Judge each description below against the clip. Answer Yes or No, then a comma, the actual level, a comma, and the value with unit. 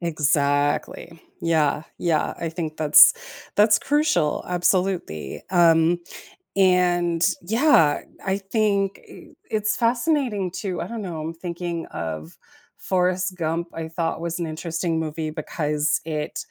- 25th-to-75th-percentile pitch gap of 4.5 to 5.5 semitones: No, average, 3.2 semitones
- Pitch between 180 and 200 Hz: No, medium, 170 Hz